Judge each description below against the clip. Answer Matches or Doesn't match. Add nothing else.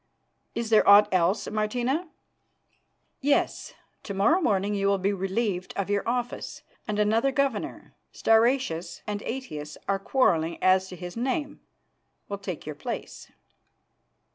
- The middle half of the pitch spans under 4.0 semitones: Doesn't match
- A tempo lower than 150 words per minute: Matches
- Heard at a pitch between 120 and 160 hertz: Doesn't match